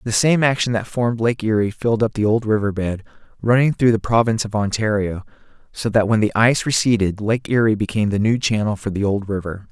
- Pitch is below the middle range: Yes, low, 110 Hz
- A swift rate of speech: Yes, fast, 215 wpm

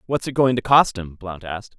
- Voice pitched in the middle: No, low, 110 Hz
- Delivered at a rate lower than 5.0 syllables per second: No, 5.5 syllables/s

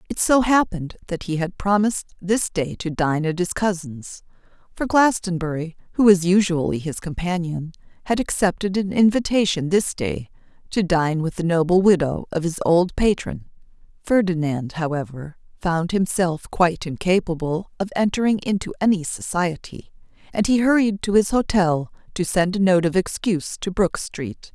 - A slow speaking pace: No, average, 155 wpm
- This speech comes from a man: No, female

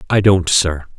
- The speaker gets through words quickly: No, average, 180 wpm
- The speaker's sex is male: Yes, male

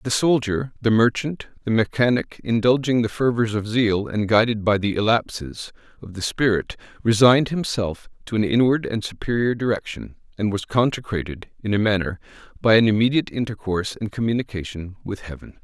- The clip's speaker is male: Yes, male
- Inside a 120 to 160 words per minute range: Yes, average, 155 wpm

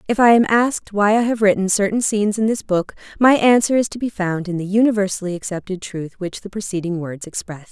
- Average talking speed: No, fast, 225 wpm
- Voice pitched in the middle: No, high, 200 Hz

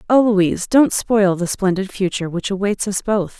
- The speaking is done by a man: No, female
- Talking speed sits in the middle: Yes, average, 195 wpm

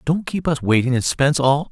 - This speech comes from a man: Yes, male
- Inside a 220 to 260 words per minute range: Yes, fast, 245 wpm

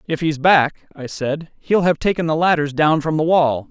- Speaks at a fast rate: Yes, fast, 225 wpm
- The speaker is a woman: No, male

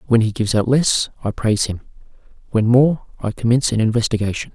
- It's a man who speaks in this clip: Yes, male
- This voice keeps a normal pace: Yes, average, 185 wpm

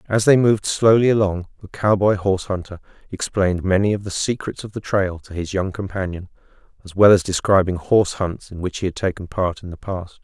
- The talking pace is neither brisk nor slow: No, fast, 210 wpm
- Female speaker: No, male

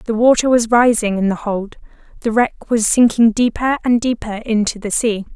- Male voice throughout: No, female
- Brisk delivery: No, average, 190 wpm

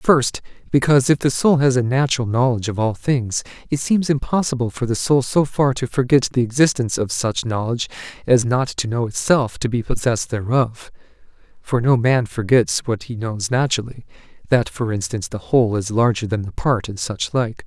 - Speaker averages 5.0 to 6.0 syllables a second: Yes, 5.4 syllables/s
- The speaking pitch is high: No, low, 120 Hz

